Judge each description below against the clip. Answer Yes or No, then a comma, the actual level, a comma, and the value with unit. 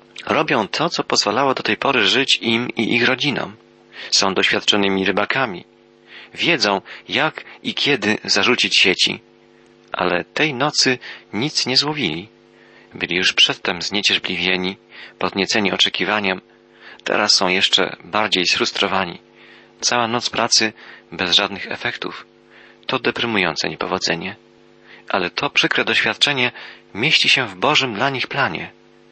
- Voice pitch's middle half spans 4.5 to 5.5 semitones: No, average, 3.9 semitones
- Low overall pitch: Yes, low, 100 Hz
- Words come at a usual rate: Yes, average, 120 wpm